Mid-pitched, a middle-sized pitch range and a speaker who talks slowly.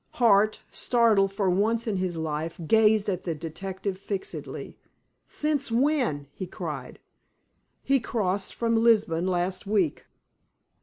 No: high, 200 Hz; average, 3.9 semitones; slow, 120 wpm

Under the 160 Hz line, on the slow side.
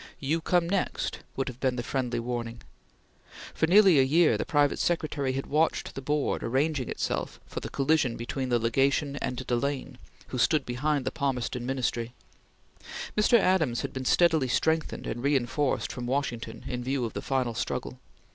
No: low, 135 Hz; average, 170 wpm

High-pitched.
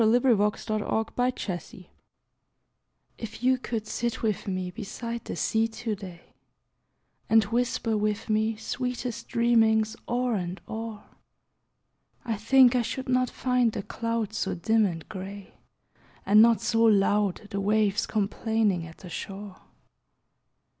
Yes: high, 220 Hz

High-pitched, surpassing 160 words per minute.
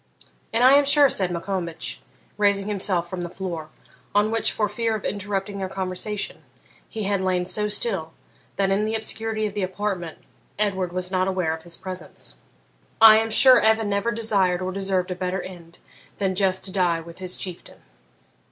Yes: high, 195 Hz; average, 180 wpm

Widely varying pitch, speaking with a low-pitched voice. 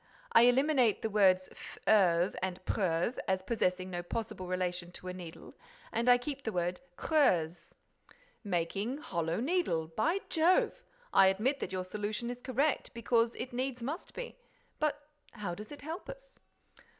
No: wide, 6.6 semitones; high, 215 Hz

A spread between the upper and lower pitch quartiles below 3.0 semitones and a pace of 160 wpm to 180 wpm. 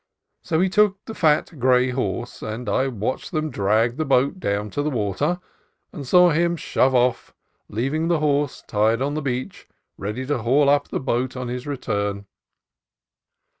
No: average, 4.5 semitones; average, 170 wpm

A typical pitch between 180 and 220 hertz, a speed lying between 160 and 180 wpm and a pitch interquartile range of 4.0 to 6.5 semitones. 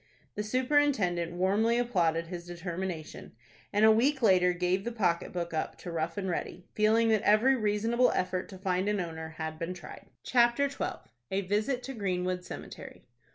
Yes: high, 190 Hz; average, 170 wpm; average, 4.3 semitones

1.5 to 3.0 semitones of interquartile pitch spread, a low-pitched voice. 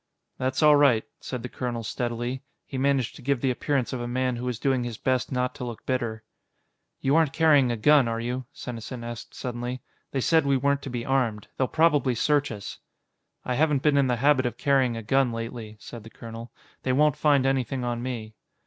Yes: narrow, 2.6 semitones; low, 125 Hz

